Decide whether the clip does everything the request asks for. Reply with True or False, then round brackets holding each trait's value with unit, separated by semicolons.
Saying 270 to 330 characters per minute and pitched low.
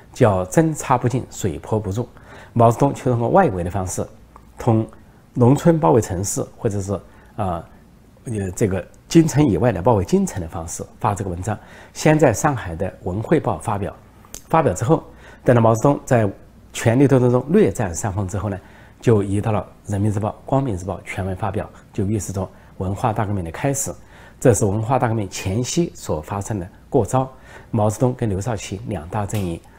True (275 characters per minute; 110 Hz)